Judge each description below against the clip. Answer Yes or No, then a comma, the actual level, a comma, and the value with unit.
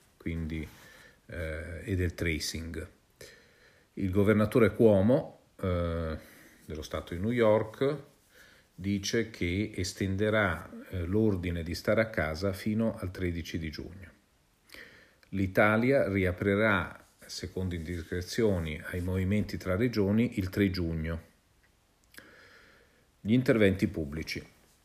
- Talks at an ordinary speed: No, slow, 100 wpm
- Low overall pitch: Yes, very low, 95 Hz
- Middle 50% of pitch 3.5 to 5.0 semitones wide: Yes, average, 3.9 semitones